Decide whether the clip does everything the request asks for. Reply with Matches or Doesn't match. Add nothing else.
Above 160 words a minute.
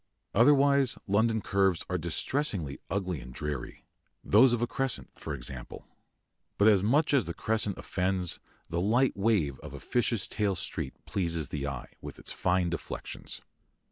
Doesn't match